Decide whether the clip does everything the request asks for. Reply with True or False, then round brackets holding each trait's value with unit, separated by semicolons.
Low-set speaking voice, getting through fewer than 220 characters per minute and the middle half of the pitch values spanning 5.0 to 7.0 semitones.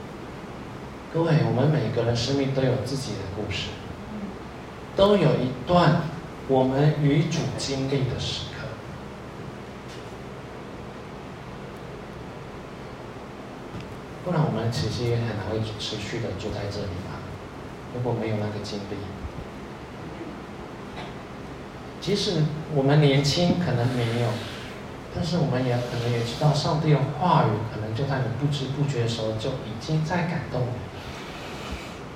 True (125 Hz; 185 characters per minute; 5.3 semitones)